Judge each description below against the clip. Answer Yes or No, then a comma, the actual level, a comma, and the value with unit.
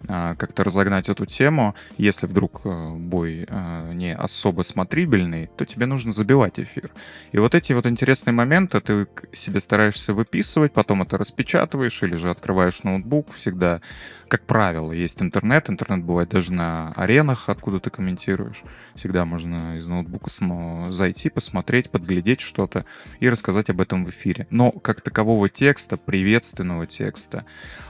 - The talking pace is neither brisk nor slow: Yes, average, 140 wpm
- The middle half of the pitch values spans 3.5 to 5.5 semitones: Yes, average, 4.4 semitones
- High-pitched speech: No, very low, 95 Hz